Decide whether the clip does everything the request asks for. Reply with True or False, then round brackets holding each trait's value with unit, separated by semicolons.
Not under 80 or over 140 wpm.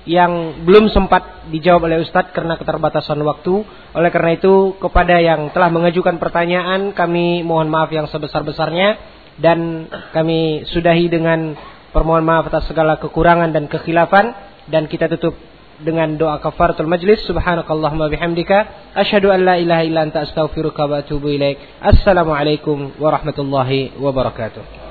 True (130 wpm)